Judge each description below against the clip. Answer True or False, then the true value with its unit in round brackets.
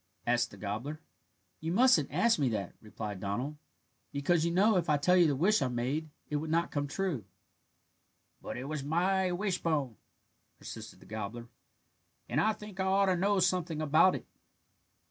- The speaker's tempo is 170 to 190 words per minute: True (175 wpm)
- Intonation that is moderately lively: False (6.5 semitones)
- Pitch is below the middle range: False (155 Hz)